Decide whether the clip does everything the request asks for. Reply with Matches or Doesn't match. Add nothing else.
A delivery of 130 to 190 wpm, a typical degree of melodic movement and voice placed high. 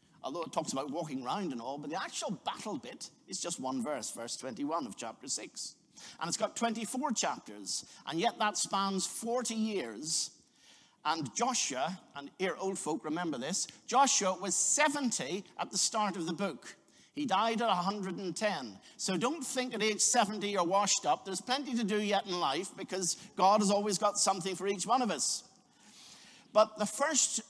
Matches